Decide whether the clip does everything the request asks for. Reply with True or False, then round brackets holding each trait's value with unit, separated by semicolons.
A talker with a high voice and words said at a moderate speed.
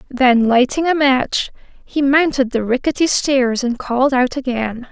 True (260 Hz; 160 wpm)